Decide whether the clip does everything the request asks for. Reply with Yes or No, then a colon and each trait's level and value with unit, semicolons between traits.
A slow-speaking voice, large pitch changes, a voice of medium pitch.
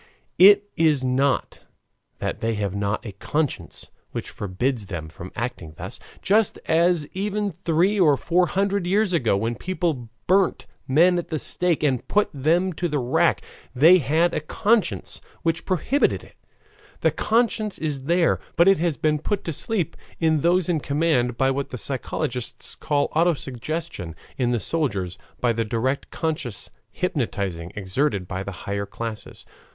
No: average, 160 wpm; wide, 6.7 semitones; medium, 150 Hz